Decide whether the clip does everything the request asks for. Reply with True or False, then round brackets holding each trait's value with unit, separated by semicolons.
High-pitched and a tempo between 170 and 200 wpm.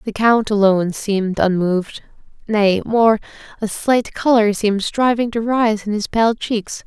False (215 Hz; 150 wpm)